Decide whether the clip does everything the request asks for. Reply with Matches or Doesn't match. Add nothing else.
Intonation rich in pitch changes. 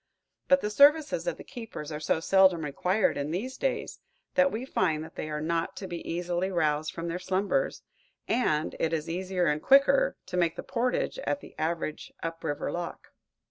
Matches